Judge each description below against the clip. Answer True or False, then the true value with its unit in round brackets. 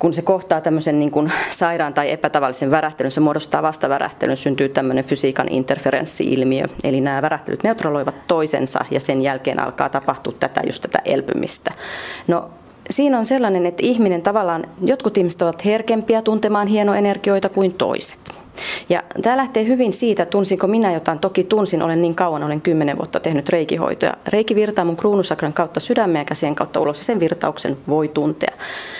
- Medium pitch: True (170 Hz)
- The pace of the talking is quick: True (160 wpm)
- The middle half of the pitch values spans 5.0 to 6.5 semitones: True (5.5 semitones)